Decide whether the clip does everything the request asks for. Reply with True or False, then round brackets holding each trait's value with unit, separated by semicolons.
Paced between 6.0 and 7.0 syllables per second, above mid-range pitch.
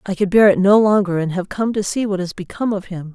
True (6.3 syllables/s; 195 Hz)